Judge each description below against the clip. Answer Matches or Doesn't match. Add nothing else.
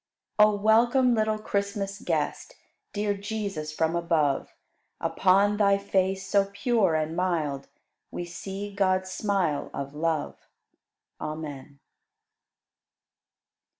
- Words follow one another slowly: Matches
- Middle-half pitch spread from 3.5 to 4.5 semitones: Matches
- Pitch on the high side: Matches